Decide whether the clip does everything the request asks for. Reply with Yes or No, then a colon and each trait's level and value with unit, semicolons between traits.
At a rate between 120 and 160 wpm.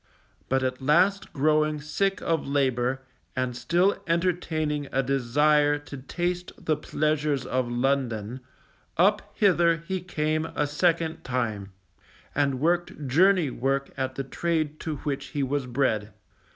Yes: slow, 135 wpm